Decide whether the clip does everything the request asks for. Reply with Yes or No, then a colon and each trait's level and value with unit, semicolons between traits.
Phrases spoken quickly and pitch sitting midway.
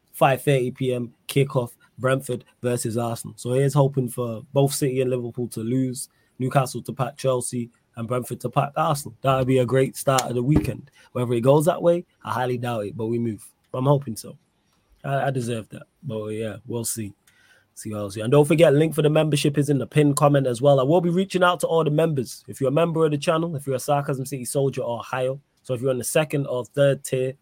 No: fast, 235 wpm; low, 130 Hz